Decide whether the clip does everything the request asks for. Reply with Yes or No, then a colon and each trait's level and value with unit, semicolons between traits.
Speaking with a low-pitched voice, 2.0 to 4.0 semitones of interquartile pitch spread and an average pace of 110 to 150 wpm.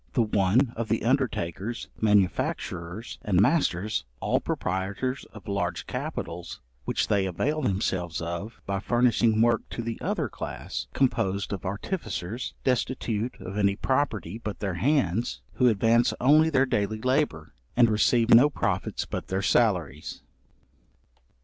No: low, 110 Hz; average, 4.4 semitones; slow, 135 wpm